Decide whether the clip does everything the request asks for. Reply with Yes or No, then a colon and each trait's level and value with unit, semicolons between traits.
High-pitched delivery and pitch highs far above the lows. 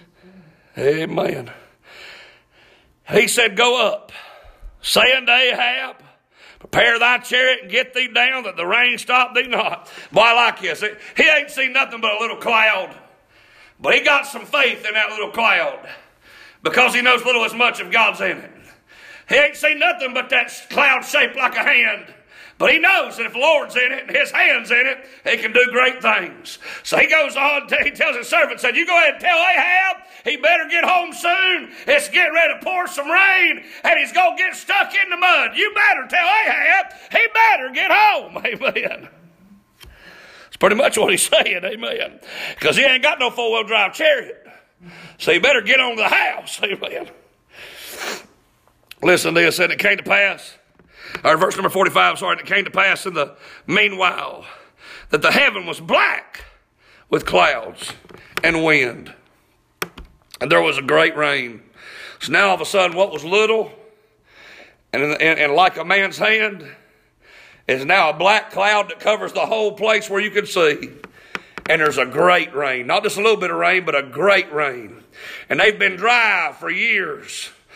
Yes: high, 245 Hz; wide, 6.5 semitones